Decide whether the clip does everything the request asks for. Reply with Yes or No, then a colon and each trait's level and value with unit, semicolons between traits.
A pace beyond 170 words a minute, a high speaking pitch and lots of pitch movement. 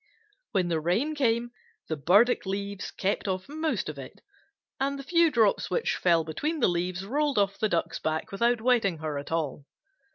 Yes: average, 185 wpm; high, 200 Hz; wide, 6.7 semitones